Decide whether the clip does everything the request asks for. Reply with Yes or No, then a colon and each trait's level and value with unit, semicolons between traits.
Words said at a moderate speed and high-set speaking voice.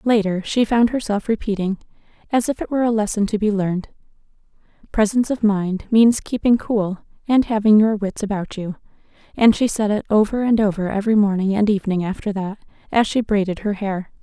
Yes: average, 185 wpm; high, 210 Hz